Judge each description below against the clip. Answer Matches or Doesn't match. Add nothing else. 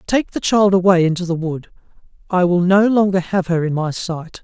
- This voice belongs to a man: Matches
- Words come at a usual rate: Doesn't match